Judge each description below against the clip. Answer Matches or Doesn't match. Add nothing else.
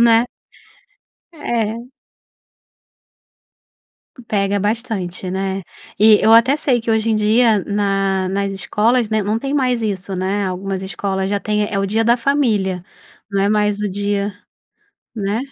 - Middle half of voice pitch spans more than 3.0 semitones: Doesn't match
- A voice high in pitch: Matches